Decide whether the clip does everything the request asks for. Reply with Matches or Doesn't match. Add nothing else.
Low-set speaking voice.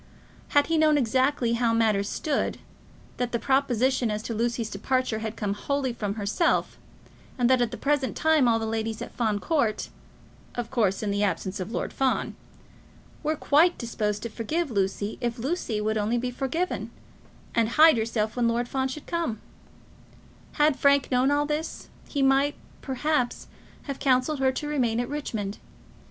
Doesn't match